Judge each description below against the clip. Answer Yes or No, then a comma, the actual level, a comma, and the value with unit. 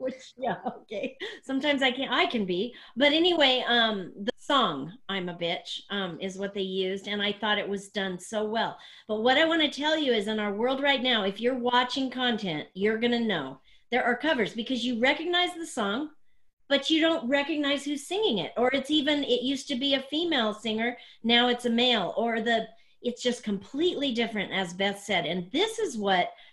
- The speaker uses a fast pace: Yes, fast, 210 wpm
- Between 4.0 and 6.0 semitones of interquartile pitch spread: Yes, average, 5.3 semitones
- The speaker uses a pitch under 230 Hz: No, high, 245 Hz